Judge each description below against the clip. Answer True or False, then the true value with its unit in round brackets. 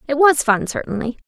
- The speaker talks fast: False (190 wpm)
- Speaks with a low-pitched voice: False (270 Hz)